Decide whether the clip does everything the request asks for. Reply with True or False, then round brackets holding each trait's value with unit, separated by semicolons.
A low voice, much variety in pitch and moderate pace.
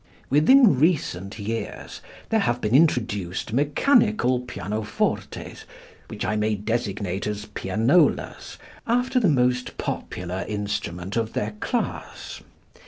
False (115 Hz; 6.2 semitones; 105 wpm)